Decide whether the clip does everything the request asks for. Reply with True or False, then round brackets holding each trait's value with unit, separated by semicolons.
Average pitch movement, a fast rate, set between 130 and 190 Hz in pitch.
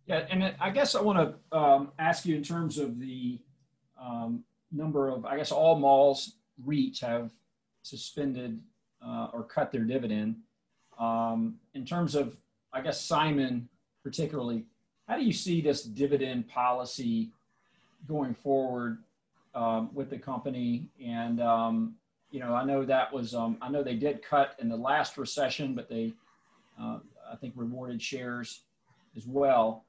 False (4.7 semitones; 155 wpm; 135 Hz)